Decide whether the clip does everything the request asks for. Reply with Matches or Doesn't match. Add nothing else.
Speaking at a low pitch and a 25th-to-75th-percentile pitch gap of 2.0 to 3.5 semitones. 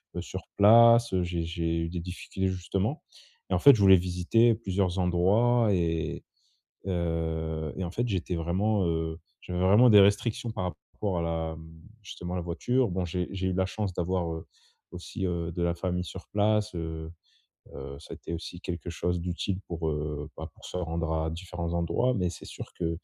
Matches